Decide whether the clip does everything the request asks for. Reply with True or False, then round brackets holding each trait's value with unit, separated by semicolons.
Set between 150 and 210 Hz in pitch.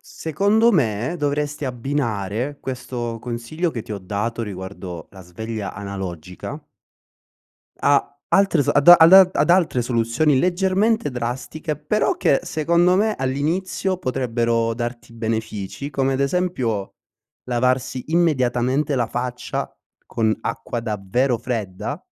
False (125 Hz)